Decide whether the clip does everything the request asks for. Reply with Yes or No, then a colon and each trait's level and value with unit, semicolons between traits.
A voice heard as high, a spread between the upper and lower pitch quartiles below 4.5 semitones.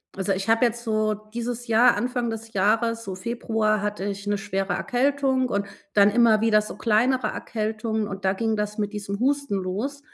Yes: high, 220 Hz; narrow, 2.5 semitones